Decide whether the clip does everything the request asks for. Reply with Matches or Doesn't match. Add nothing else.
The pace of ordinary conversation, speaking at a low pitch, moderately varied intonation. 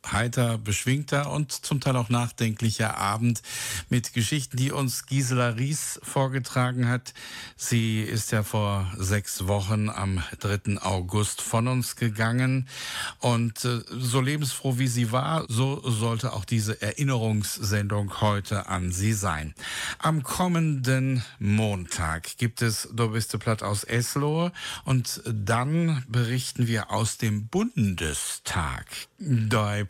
Doesn't match